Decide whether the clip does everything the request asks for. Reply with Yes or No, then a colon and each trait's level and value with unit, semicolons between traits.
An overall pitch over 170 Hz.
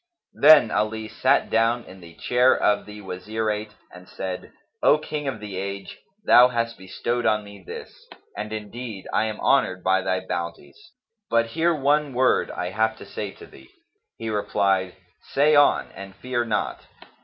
No: low, 110 Hz